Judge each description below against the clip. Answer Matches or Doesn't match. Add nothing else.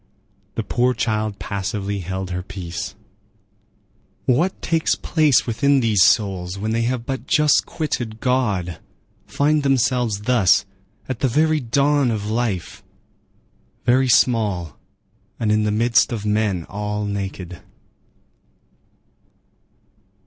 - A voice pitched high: Doesn't match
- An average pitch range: Matches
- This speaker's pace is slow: Matches